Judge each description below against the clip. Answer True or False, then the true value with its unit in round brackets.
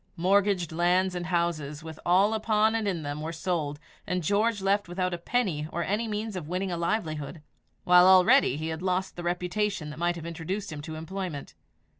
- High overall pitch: False (180 Hz)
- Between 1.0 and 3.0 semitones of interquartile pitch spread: False (3.4 semitones)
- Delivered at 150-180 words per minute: False (195 wpm)